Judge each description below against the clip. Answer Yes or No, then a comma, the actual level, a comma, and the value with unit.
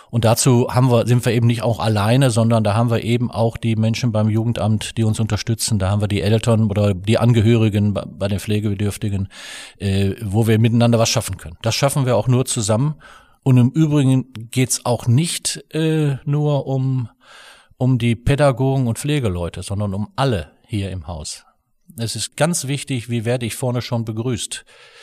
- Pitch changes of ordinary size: Yes, average, 3.1 semitones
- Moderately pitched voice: No, low, 115 Hz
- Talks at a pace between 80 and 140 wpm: No, average, 185 wpm